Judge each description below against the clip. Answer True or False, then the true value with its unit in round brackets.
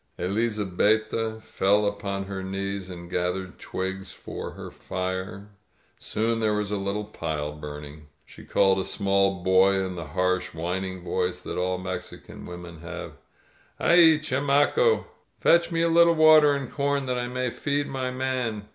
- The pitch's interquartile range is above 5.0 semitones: True (5.6 semitones)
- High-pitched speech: False (100 Hz)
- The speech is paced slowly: False (155 wpm)